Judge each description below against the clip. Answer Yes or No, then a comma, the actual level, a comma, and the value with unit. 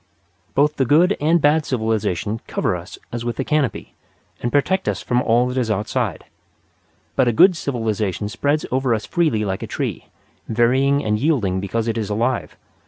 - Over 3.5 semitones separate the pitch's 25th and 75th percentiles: Yes, average, 4.8 semitones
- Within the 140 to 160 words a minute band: No, average, 175 wpm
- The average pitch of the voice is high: No, low, 120 Hz